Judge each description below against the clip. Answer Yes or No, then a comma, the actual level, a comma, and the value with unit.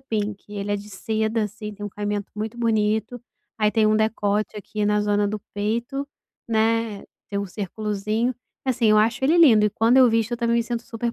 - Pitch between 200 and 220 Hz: Yes, high, 215 Hz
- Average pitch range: No, narrow, 1.8 semitones